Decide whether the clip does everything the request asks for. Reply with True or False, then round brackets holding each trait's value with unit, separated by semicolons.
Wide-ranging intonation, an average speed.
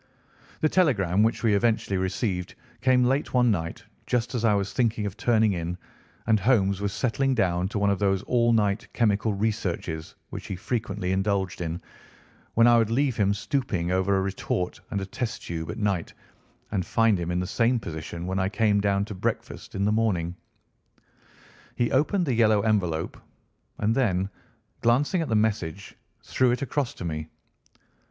False (3.8 semitones; 175 wpm)